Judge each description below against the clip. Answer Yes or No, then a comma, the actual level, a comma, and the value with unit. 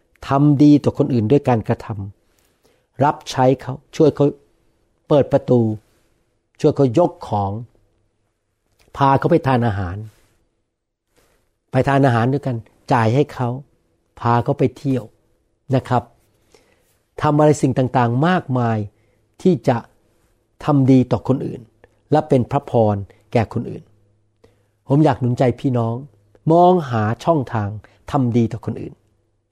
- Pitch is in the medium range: No, low, 120 Hz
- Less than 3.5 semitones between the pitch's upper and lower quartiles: No, average, 4.4 semitones